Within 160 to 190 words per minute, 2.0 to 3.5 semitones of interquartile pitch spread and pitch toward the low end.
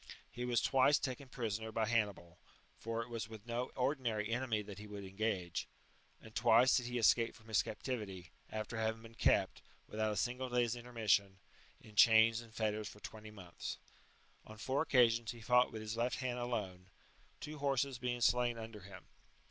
Yes: average, 180 wpm; narrow, 2.4 semitones; low, 115 Hz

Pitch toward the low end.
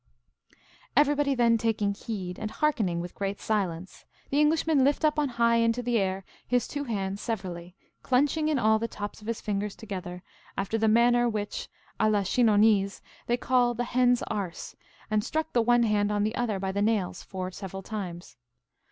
No: high, 220 Hz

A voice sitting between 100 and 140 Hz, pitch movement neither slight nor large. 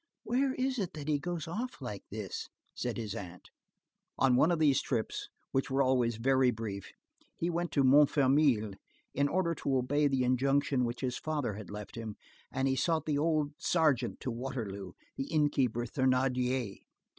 Yes: low, 135 Hz; average, 4.1 semitones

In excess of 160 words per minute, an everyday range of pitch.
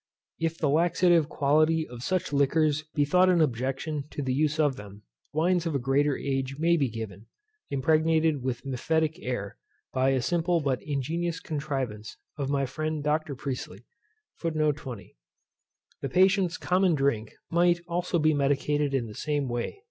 No: average, 155 wpm; average, 3.5 semitones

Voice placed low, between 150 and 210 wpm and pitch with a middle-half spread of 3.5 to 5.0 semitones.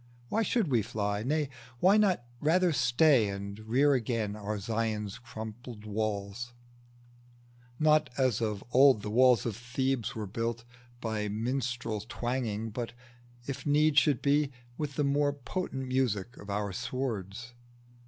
No: low, 120 Hz; average, 140 wpm; average, 4.4 semitones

